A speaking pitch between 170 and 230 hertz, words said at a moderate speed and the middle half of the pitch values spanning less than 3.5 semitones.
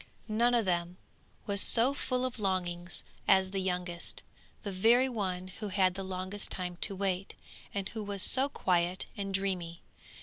Yes: high, 190 Hz; average, 165 wpm; narrow, 2.6 semitones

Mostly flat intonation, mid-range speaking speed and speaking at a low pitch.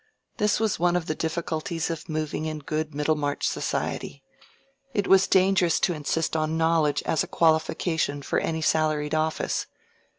No: narrow, 1.6 semitones; average, 155 wpm; medium, 160 Hz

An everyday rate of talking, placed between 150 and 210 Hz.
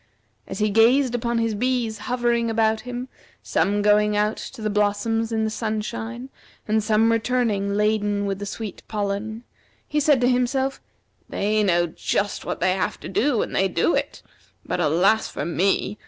No: average, 170 wpm; high, 220 Hz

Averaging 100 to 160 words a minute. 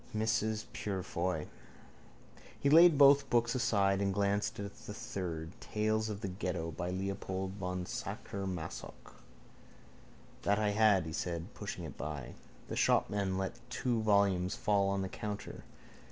Yes: average, 140 wpm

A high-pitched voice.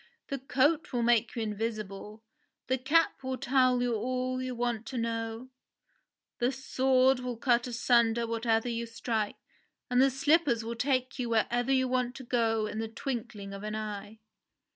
Yes: high, 240 Hz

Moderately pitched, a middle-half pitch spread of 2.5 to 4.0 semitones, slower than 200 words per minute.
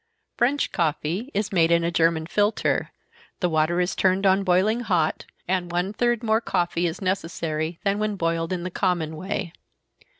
Yes: medium, 180 Hz; average, 3.3 semitones; average, 170 wpm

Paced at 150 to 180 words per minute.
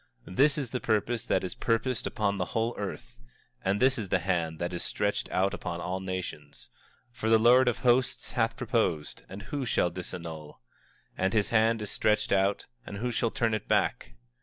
No: average, 200 wpm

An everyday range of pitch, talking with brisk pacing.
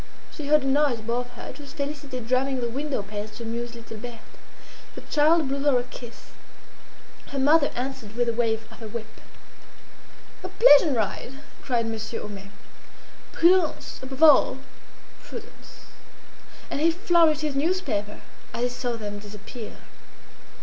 No: average, 4.5 semitones; average, 150 wpm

